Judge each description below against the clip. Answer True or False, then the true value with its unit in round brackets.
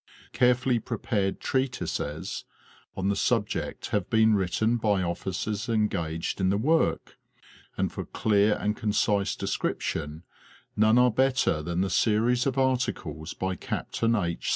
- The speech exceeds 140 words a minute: False (135 wpm)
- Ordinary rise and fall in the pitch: True (4.2 semitones)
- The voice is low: True (105 Hz)